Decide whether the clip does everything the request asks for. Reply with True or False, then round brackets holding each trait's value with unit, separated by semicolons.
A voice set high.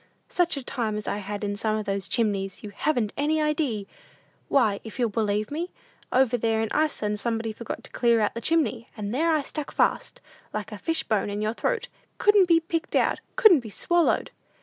True (235 Hz)